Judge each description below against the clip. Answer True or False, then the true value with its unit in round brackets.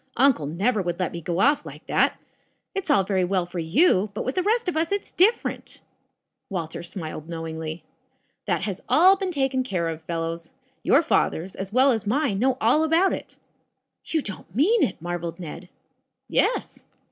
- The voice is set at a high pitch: True (195 Hz)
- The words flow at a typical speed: True (180 wpm)